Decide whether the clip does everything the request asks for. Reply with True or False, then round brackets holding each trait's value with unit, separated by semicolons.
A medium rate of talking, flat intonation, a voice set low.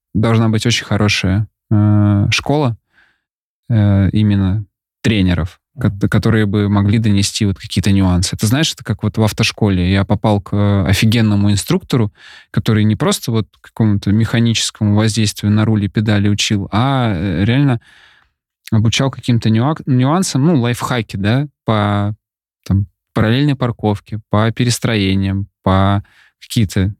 True (125 wpm; 2.3 semitones; 105 Hz)